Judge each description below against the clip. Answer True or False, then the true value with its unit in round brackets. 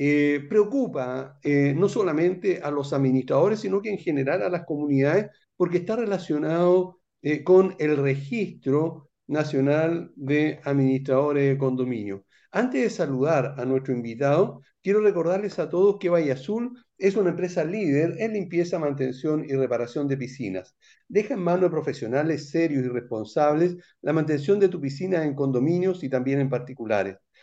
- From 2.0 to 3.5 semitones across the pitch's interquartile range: False (5.0 semitones)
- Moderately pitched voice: True (150 Hz)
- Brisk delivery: False (155 wpm)